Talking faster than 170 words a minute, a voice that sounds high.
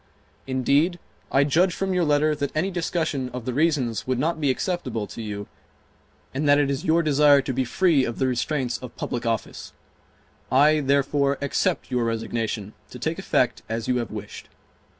No: average, 180 wpm; medium, 140 Hz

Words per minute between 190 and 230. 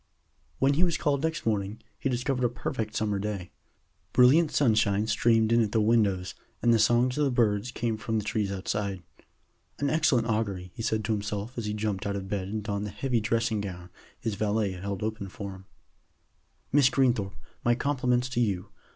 Yes: average, 195 wpm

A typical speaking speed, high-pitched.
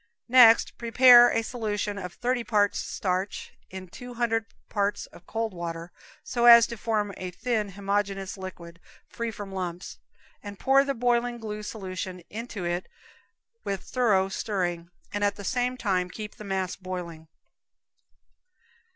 Yes: average, 150 wpm; high, 205 Hz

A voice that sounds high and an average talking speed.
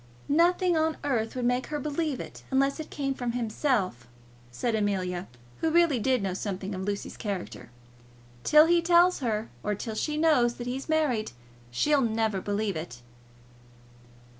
Yes: high, 245 Hz; average, 160 wpm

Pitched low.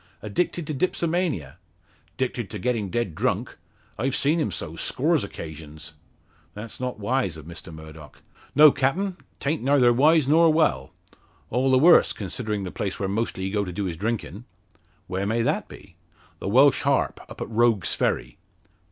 Yes: low, 115 Hz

